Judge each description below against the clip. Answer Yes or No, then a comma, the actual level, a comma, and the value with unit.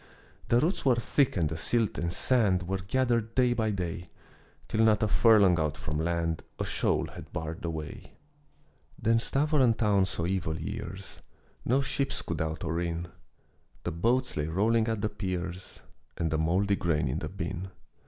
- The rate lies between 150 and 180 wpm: Yes, average, 175 wpm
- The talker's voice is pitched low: Yes, very low, 95 Hz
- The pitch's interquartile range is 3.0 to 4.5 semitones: No, wide, 5.5 semitones